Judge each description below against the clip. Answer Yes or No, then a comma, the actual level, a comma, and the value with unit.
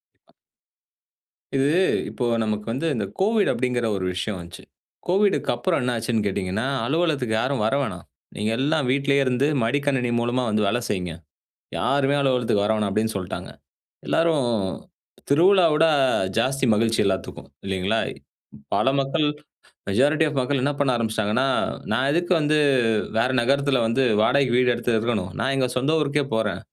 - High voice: No, low, 125 Hz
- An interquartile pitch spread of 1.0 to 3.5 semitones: No, average, 4.3 semitones